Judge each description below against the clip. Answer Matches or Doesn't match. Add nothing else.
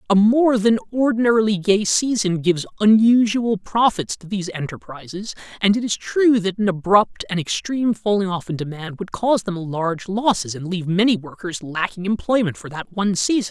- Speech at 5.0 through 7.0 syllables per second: Matches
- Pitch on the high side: Matches